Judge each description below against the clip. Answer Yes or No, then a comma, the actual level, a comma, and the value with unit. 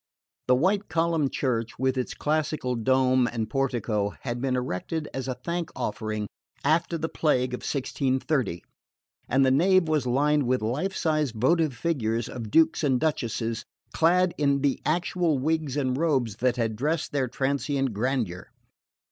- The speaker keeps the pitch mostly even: No, average, 4.1 semitones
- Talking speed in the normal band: Yes, average, 155 wpm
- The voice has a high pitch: No, low, 135 Hz